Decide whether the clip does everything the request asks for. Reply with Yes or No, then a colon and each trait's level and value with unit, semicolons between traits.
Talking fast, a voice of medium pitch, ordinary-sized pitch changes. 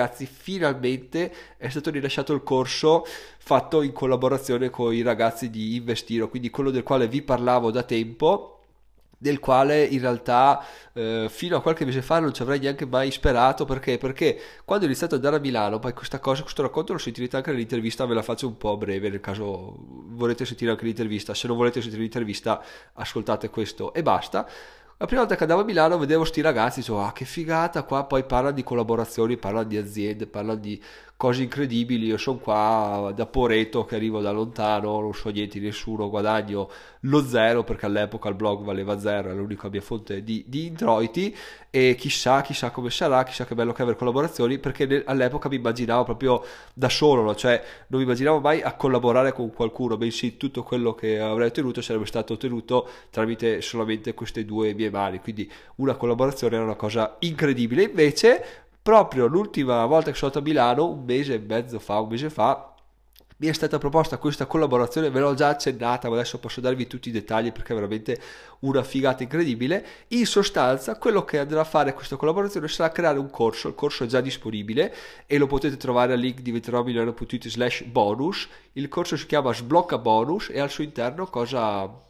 No: fast, 190 wpm; low, 125 Hz; average, 3.8 semitones